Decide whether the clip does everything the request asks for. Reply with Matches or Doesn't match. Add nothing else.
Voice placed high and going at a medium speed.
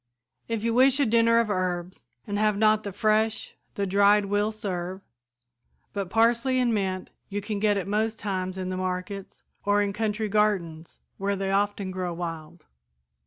Matches